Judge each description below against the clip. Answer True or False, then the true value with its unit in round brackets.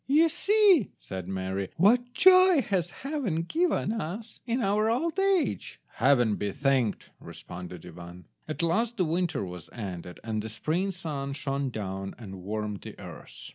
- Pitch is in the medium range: True (155 Hz)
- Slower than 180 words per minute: True (155 wpm)